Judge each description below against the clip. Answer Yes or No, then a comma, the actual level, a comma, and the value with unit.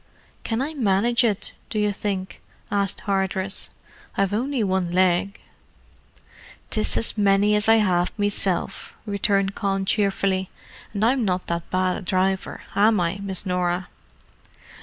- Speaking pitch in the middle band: No, high, 195 Hz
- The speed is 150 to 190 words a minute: No, average, 140 wpm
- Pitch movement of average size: No, narrow, 1.9 semitones